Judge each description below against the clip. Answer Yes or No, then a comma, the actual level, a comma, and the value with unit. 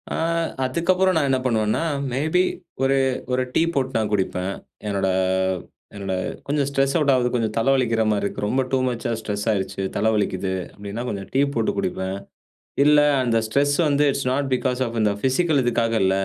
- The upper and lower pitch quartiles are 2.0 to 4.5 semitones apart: No, average, 4.9 semitones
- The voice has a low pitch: Yes, low, 120 Hz